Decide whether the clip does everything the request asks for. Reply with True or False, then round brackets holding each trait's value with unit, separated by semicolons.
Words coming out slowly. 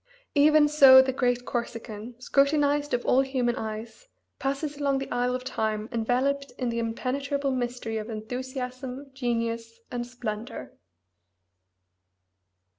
True (120 wpm)